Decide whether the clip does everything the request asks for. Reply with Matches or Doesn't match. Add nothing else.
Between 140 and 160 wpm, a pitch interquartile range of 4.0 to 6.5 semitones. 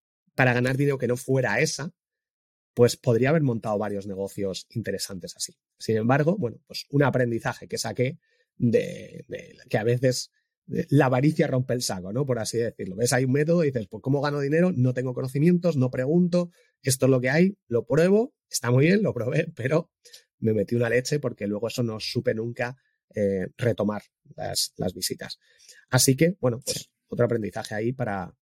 Doesn't match